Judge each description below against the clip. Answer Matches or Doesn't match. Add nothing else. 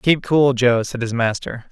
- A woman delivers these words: Doesn't match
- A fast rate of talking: Matches